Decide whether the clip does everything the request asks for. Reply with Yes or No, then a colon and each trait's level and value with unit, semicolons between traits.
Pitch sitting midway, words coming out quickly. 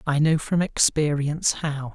No: medium, 150 Hz; average, 155 wpm